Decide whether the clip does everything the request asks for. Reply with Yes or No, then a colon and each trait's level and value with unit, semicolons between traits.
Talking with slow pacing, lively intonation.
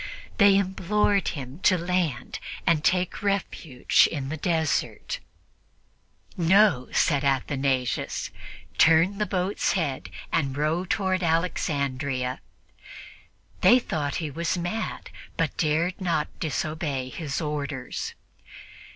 No: slow, 105 wpm; average, 4.7 semitones